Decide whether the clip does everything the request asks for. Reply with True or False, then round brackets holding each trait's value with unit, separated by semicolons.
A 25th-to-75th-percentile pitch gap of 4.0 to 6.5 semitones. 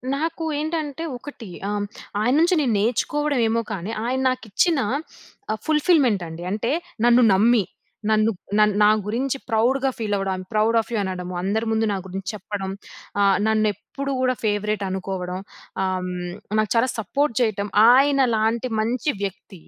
True (4.4 semitones)